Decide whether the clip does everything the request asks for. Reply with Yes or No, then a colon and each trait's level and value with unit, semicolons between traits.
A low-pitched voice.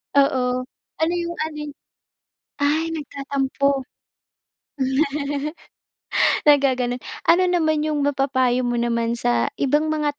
No: very high, 280 Hz